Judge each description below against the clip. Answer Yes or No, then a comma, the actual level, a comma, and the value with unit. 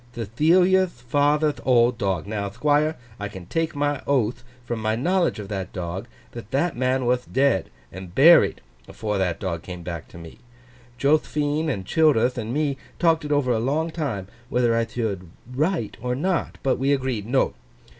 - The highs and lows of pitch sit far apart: Yes, wide, 6.2 semitones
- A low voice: Yes, low, 125 Hz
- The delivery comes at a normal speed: Yes, average, 165 wpm